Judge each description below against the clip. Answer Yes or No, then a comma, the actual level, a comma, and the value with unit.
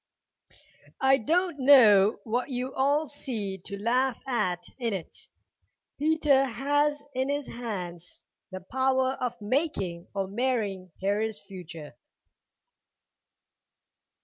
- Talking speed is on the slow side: Yes, slow, 105 wpm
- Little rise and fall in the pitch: No, wide, 5.4 semitones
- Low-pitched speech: No, high, 245 Hz